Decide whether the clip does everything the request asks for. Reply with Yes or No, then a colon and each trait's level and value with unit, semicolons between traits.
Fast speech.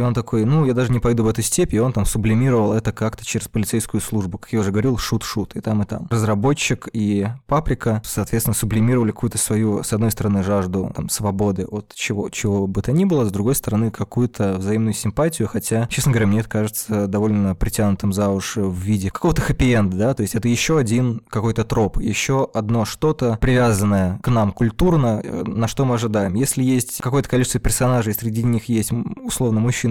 Yes: fast, 195 wpm